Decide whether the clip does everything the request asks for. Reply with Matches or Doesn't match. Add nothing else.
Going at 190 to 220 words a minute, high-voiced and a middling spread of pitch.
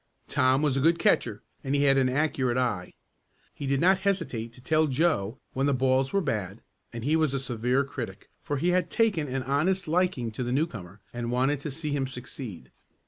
Doesn't match